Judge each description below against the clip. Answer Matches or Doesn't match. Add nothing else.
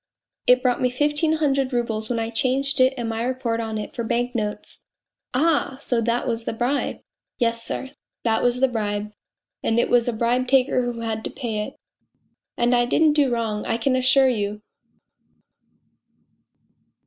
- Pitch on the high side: Matches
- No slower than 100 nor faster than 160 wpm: Doesn't match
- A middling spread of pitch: Doesn't match